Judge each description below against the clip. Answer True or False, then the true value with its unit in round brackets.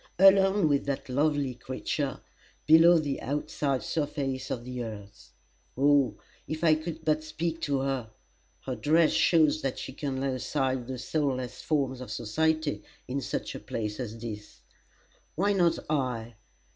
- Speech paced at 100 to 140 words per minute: False (150 wpm)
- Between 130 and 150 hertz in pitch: True (140 Hz)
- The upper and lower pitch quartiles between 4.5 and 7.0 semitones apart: False (3.7 semitones)